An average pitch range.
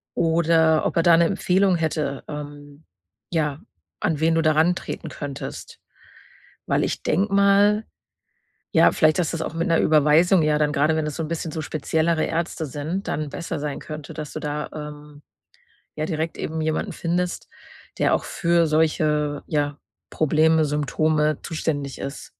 No: narrow, 1.9 semitones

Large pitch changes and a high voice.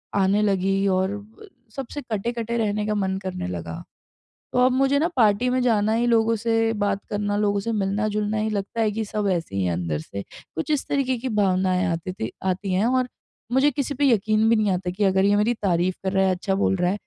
No: average, 3.2 semitones; high, 205 Hz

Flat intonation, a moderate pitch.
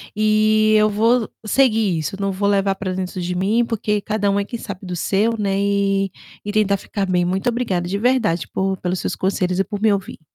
No: narrow, 2.2 semitones; high, 200 Hz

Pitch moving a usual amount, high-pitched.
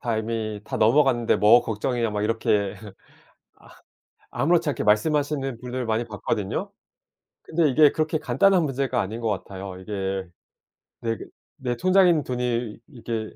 No: average, 4.6 semitones; low, 120 Hz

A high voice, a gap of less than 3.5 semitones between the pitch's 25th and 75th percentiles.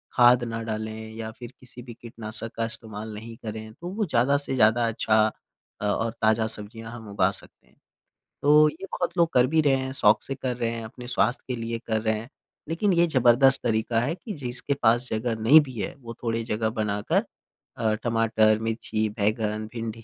No: low, 115 Hz; narrow, 2.5 semitones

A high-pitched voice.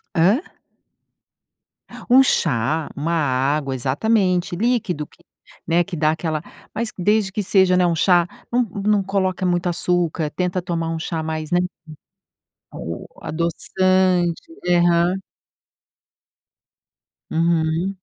No: medium, 175 Hz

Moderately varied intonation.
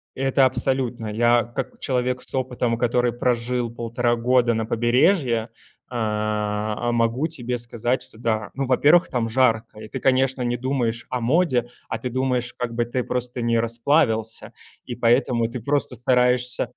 No: narrow, 1.8 semitones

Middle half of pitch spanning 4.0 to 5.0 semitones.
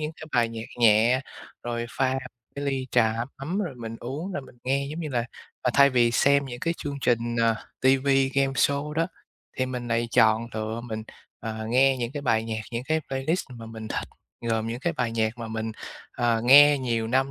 No: average, 3.2 semitones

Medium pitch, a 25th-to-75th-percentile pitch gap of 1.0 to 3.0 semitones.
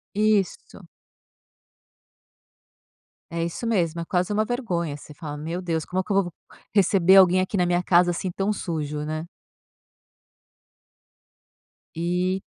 Yes: medium, 180 Hz; narrow, 2.6 semitones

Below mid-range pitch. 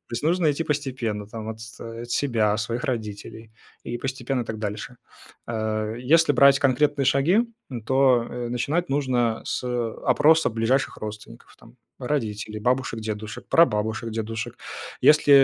Yes: low, 120 Hz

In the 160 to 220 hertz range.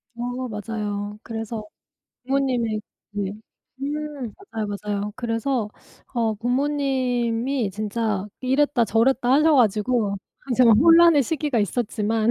No: high, 235 Hz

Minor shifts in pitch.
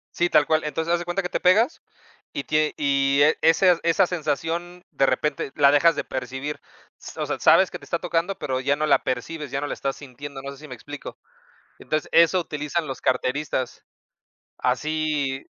No: average, 3.2 semitones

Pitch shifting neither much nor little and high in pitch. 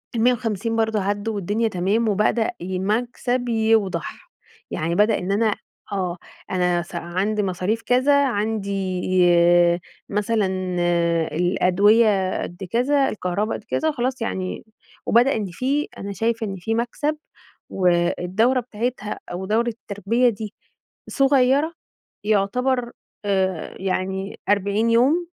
Yes: average, 3.8 semitones; high, 215 Hz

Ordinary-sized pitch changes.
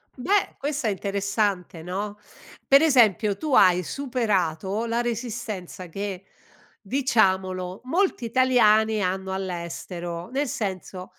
Yes: average, 4.6 semitones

